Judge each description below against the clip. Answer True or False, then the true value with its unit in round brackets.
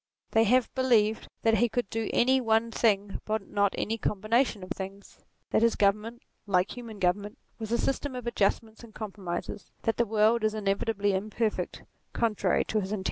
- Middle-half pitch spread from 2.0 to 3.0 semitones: True (2.4 semitones)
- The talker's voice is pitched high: True (220 Hz)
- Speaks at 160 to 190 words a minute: True (180 wpm)